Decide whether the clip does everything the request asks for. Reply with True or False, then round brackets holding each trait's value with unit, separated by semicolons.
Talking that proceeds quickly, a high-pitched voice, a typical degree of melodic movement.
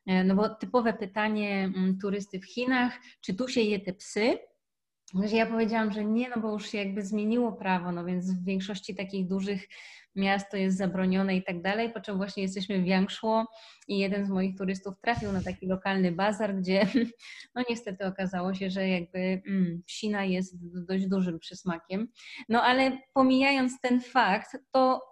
True (165 wpm; 200 Hz; 3.1 semitones)